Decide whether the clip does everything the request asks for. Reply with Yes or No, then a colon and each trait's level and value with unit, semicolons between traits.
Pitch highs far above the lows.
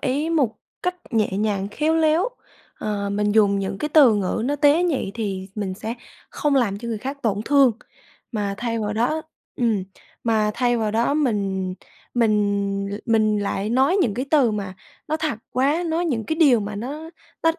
Yes: wide, 5.8 semitones